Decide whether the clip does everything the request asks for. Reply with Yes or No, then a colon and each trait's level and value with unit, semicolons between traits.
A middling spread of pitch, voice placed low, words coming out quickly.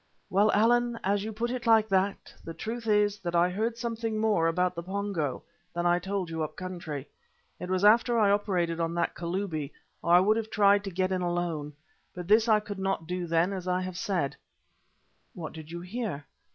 No: average, 3.6 semitones; medium, 185 Hz; fast, 215 wpm